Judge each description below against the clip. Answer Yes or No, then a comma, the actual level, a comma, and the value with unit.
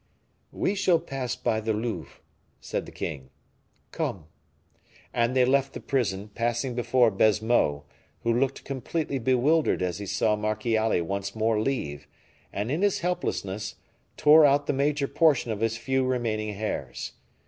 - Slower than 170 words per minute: Yes, average, 150 wpm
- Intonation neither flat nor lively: Yes, average, 4.3 semitones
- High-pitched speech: No, low, 120 Hz